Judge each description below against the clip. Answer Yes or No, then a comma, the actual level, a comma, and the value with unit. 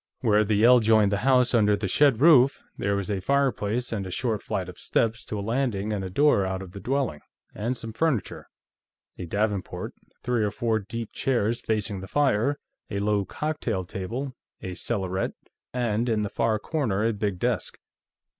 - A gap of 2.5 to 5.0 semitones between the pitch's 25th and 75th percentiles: Yes, average, 3.6 semitones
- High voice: No, low, 110 Hz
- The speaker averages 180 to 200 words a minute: Yes, average, 185 wpm